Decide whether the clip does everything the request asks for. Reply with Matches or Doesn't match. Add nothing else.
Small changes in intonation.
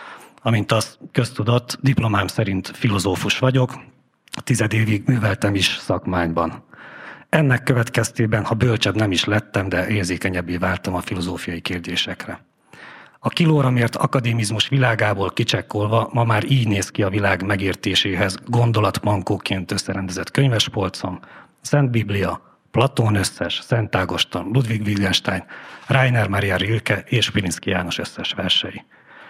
Doesn't match